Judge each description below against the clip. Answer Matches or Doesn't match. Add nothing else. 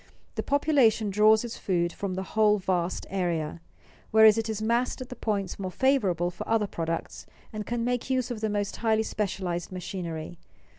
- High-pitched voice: Matches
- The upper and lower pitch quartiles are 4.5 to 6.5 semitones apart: Doesn't match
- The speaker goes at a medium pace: Matches